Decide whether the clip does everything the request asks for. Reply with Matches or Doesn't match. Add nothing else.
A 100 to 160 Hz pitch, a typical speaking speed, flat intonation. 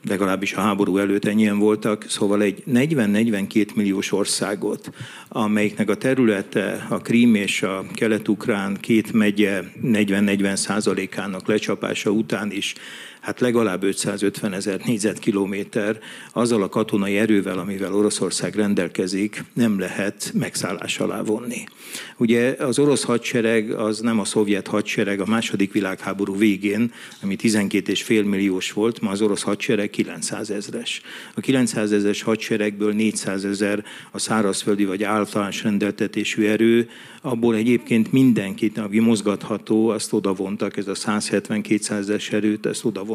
Matches